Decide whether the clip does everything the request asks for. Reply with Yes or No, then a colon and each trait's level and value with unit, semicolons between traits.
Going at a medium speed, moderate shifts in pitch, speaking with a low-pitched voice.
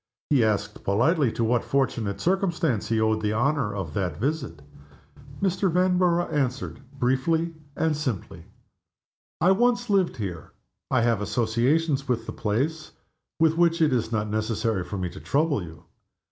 No: average, 150 wpm; wide, 7.1 semitones; low, 125 Hz